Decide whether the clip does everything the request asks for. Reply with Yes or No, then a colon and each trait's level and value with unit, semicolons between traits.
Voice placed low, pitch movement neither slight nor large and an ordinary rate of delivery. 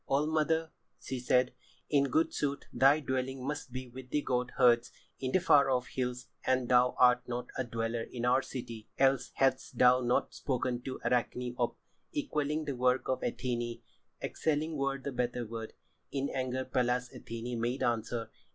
No: low, 125 Hz; narrow, 1.9 semitones; average, 170 wpm